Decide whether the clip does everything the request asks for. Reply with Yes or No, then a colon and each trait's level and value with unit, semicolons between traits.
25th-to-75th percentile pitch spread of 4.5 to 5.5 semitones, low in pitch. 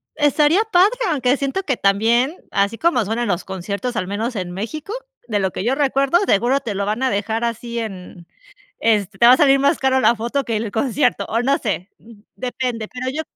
No: average, 4.8 semitones; high, 235 Hz